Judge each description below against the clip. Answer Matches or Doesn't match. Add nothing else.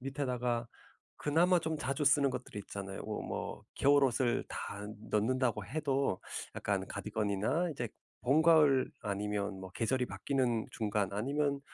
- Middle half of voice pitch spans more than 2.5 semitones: Matches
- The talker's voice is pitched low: Matches